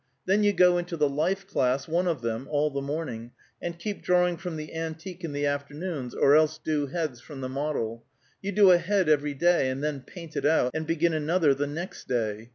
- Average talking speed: No, fast, 220 wpm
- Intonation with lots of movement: No, average, 3.9 semitones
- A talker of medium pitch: Yes, medium, 155 Hz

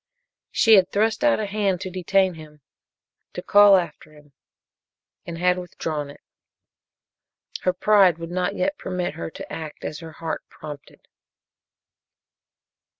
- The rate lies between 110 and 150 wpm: Yes, average, 140 wpm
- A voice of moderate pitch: Yes, medium, 180 Hz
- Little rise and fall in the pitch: No, average, 3.7 semitones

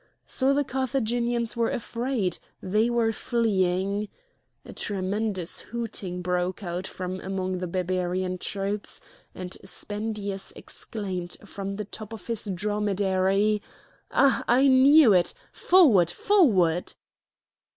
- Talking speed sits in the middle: No, slow, 110 wpm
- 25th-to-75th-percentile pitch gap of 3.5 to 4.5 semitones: Yes, average, 3.9 semitones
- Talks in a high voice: Yes, high, 205 Hz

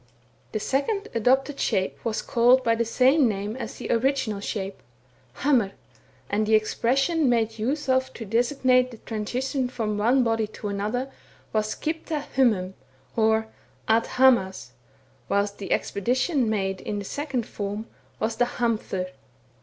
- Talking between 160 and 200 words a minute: No, average, 145 wpm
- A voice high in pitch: Yes, high, 230 Hz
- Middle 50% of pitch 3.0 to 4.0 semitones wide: Yes, average, 3.6 semitones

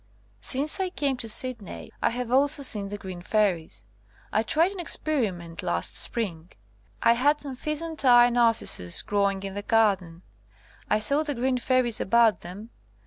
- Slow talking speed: No, average, 160 wpm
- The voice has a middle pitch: No, high, 230 Hz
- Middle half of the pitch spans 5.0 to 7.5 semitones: Yes, wide, 5.4 semitones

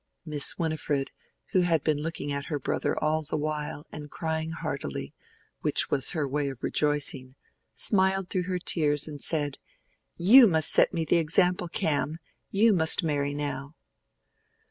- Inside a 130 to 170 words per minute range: Yes, average, 155 wpm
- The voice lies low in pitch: No, medium, 155 Hz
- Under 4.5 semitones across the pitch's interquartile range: Yes, narrow, 2.6 semitones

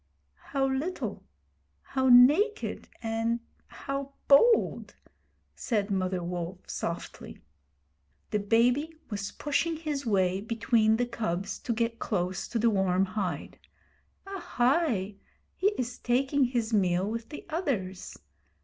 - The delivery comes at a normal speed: No, slow, 115 wpm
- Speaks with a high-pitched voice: Yes, high, 230 Hz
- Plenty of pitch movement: Yes, wide, 5.9 semitones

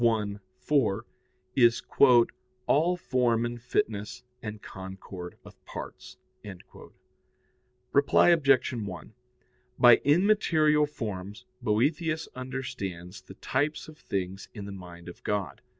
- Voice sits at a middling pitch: No, low, 115 Hz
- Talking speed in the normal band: No, slow, 105 wpm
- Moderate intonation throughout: No, wide, 6.8 semitones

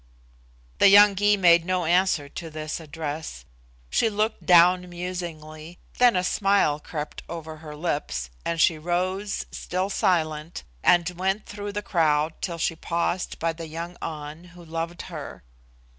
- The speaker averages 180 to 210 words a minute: No, average, 150 wpm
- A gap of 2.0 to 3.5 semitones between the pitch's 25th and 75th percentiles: Yes, average, 2.9 semitones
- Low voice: No, medium, 170 Hz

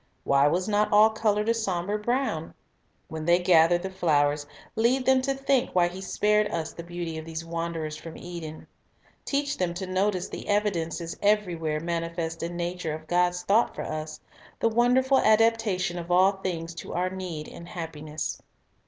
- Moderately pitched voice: Yes, medium, 175 Hz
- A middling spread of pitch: Yes, average, 4.1 semitones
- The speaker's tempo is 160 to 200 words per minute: Yes, average, 175 wpm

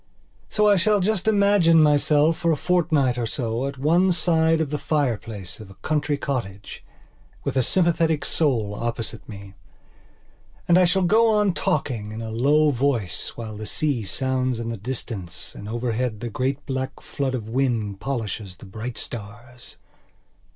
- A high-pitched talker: No, low, 130 Hz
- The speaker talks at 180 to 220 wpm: No, average, 165 wpm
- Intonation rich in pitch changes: Yes, wide, 6.1 semitones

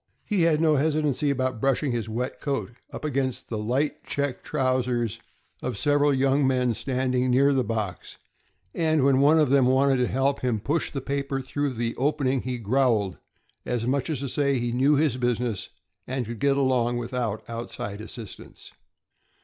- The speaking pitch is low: Yes, low, 130 Hz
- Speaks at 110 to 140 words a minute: No, average, 175 wpm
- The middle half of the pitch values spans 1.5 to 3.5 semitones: Yes, narrow, 2.6 semitones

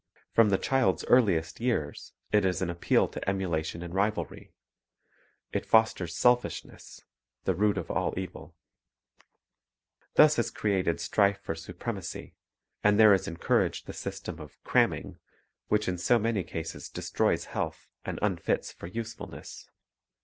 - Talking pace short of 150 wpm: Yes, average, 140 wpm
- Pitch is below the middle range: Yes, very low, 95 Hz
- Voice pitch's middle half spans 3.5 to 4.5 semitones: Yes, average, 4.0 semitones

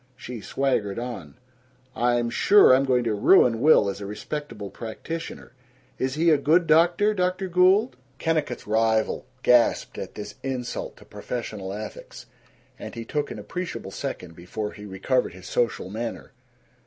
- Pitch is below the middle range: Yes, low, 120 Hz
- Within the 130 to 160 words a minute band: Yes, average, 150 wpm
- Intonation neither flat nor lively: No, wide, 6.5 semitones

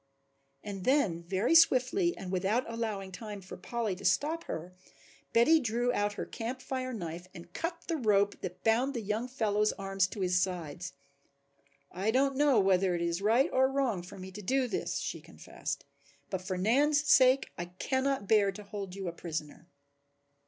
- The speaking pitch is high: Yes, high, 210 Hz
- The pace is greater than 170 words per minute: Yes, average, 180 wpm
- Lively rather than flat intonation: Yes, wide, 5.7 semitones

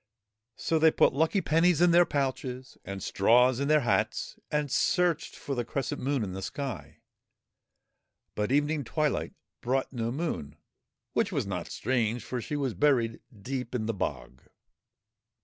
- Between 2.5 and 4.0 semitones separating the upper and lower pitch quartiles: No, average, 4.5 semitones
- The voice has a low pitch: Yes, low, 130 Hz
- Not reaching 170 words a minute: Yes, average, 155 wpm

